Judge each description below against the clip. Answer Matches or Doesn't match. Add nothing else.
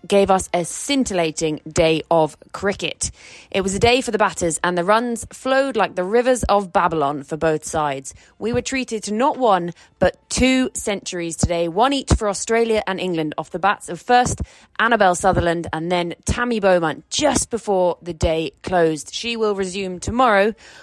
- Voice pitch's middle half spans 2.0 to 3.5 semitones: Doesn't match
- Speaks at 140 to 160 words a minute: Doesn't match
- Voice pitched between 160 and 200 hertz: Matches